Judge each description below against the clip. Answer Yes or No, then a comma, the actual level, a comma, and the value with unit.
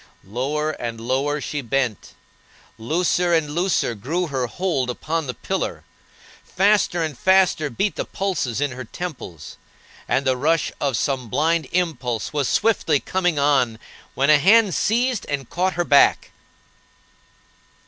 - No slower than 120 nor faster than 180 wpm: Yes, average, 140 wpm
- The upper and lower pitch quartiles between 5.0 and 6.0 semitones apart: Yes, wide, 5.4 semitones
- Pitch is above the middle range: No, medium, 150 Hz